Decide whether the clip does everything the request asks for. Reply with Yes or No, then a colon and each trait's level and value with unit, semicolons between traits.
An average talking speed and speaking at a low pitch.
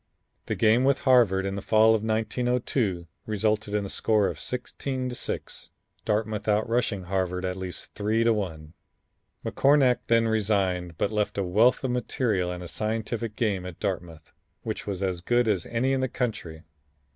Yes: average, 175 wpm; low, 110 Hz